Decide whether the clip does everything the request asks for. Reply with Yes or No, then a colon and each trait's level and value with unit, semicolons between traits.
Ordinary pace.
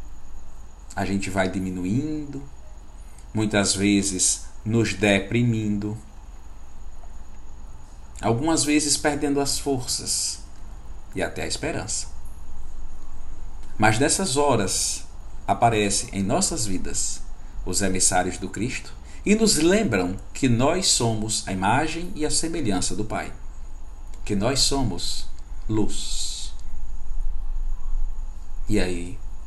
No: slow, 95 wpm